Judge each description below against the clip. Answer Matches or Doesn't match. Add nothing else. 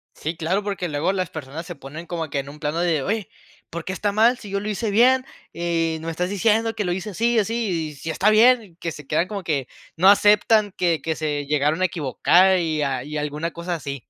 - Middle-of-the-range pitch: Matches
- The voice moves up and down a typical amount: Matches